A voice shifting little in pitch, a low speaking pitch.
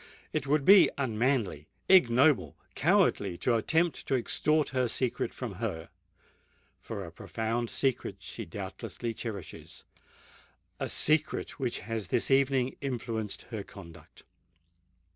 No: average, 3.8 semitones; low, 125 Hz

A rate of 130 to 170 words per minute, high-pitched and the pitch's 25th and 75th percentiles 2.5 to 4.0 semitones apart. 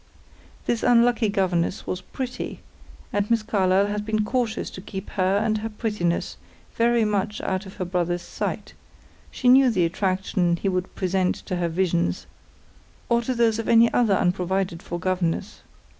Yes: average, 160 wpm; high, 195 Hz; average, 3.5 semitones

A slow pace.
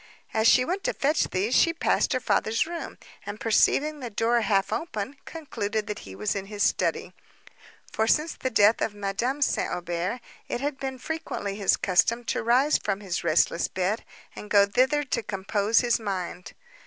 No: average, 180 wpm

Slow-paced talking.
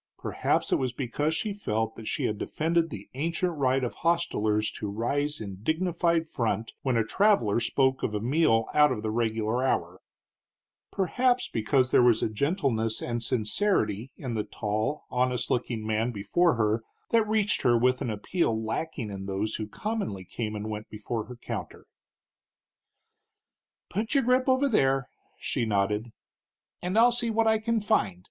No: average, 165 wpm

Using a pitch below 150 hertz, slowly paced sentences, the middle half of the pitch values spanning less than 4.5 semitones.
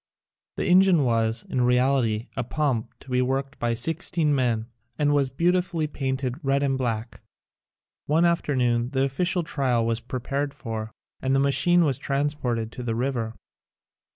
No: low, 135 Hz; average, 155 wpm; average, 3.6 semitones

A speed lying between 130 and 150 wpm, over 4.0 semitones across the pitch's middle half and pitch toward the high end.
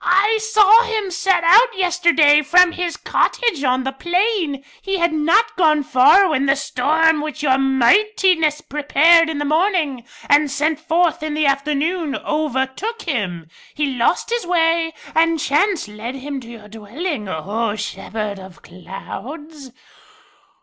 Yes: average, 145 wpm; average, 5.0 semitones; very high, 305 Hz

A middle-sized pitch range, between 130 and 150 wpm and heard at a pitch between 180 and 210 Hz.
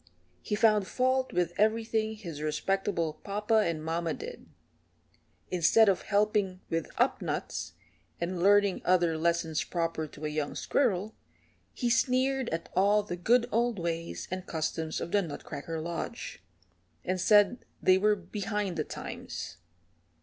Yes: average, 4.2 semitones; average, 140 wpm; high, 190 Hz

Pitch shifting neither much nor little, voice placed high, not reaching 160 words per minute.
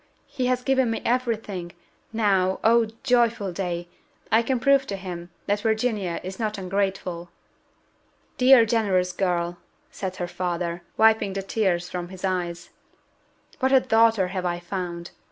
Yes: average, 4.1 semitones; high, 195 Hz; average, 150 wpm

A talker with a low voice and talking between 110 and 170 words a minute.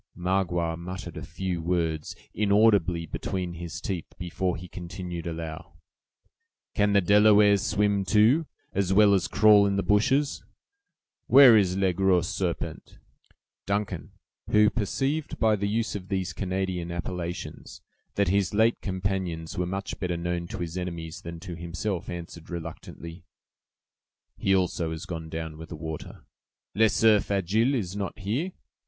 Yes: very low, 95 Hz; average, 145 wpm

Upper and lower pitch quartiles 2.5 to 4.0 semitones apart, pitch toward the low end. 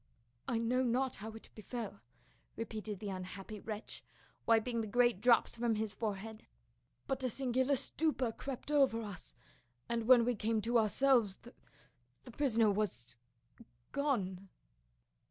No: average, 3.2 semitones; high, 225 Hz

